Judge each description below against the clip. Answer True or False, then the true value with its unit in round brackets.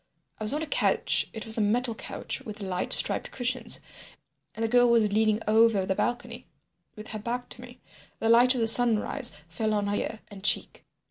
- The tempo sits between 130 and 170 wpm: False (195 wpm)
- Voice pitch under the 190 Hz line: False (225 Hz)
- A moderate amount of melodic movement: False (2.3 semitones)